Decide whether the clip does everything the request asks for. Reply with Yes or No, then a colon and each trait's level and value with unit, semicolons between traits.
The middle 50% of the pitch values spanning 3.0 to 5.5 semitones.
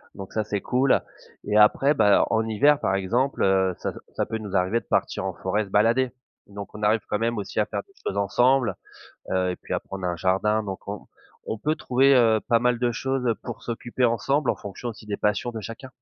Yes: average, 3.5 semitones